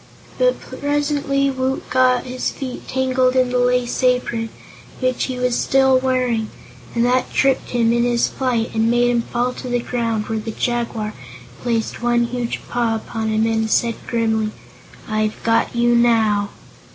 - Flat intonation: Yes, narrow, 2.0 semitones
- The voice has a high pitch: Yes, high, 240 Hz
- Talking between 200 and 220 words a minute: No, average, 165 wpm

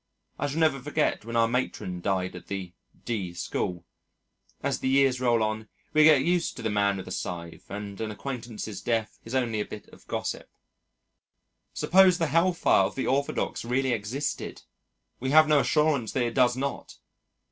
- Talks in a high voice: No, low, 120 Hz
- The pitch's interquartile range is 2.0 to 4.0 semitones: No, average, 5.1 semitones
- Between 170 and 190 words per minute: Yes, average, 180 wpm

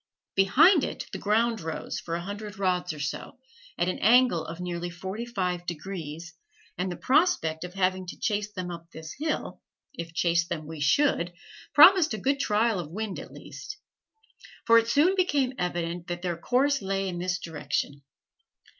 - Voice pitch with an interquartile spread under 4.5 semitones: No, average, 5.2 semitones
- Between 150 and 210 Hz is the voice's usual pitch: Yes, medium, 185 Hz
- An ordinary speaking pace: Yes, average, 175 wpm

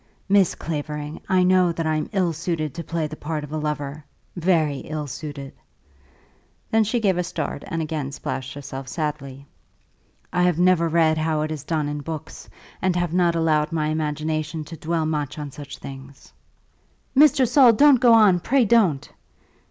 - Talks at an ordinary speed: Yes, average, 175 wpm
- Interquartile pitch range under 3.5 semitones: Yes, average, 3.1 semitones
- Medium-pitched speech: Yes, medium, 160 Hz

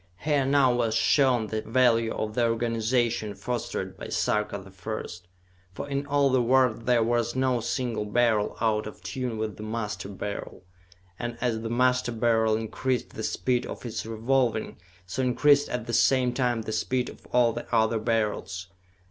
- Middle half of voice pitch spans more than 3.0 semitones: No, narrow, 2.5 semitones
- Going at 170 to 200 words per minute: Yes, average, 175 wpm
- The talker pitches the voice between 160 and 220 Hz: No, low, 115 Hz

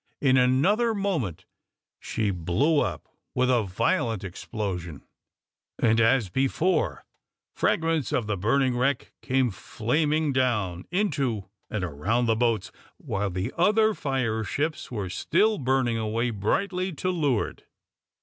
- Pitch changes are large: Yes, wide, 6.3 semitones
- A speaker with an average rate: No, slow, 125 wpm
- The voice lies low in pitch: Yes, low, 125 Hz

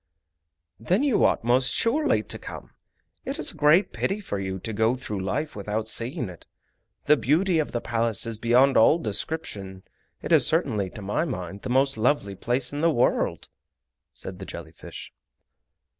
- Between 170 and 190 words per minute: Yes, average, 175 wpm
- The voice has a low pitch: Yes, low, 120 Hz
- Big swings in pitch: Yes, wide, 6.6 semitones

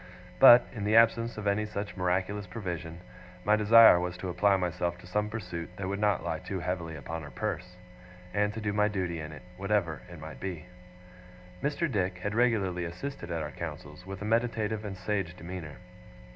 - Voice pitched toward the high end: No, very low, 95 Hz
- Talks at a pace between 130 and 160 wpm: No, average, 190 wpm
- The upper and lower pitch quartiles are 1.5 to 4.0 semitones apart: Yes, average, 3.3 semitones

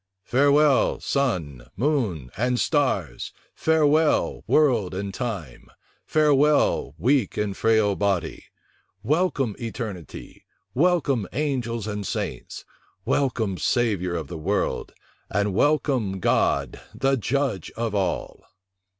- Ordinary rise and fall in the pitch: No, wide, 6.6 semitones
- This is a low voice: Yes, low, 115 Hz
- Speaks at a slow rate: Yes, slow, 100 wpm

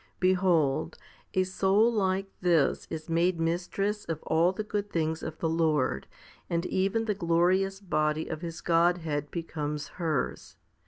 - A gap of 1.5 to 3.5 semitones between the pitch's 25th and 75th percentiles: Yes, average, 2.9 semitones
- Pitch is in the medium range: Yes, medium, 170 Hz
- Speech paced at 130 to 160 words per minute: Yes, average, 145 wpm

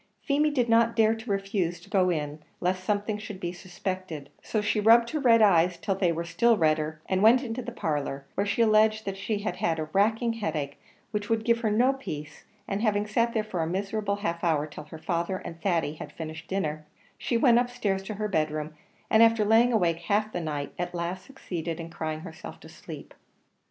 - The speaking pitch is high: Yes, high, 195 Hz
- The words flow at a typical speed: No, fast, 220 wpm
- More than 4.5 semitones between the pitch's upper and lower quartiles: Yes, average, 5.0 semitones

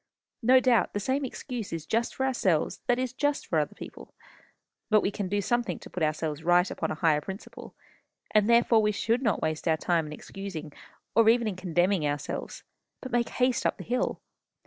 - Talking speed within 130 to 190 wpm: No, average, 200 wpm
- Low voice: No, high, 205 Hz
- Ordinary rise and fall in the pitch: No, wide, 6.4 semitones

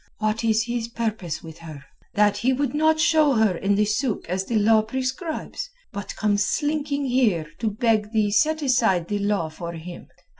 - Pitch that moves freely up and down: No, average, 4.7 semitones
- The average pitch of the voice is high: Yes, high, 220 Hz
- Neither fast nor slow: Yes, average, 180 wpm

